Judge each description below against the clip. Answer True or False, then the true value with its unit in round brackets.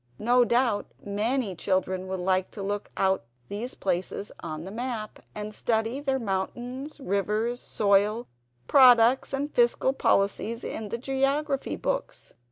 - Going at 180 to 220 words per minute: False (135 wpm)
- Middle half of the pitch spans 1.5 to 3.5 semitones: False (4.4 semitones)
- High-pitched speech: True (225 Hz)